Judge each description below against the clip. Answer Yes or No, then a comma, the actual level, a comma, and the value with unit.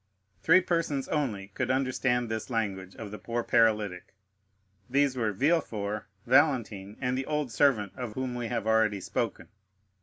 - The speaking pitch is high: No, low, 120 Hz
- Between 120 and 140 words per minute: No, average, 150 wpm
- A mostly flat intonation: No, average, 4.2 semitones